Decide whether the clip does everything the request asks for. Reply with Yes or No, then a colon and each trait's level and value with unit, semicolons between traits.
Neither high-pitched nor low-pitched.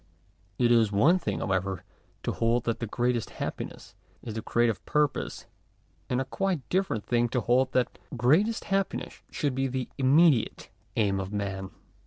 No: low, 120 Hz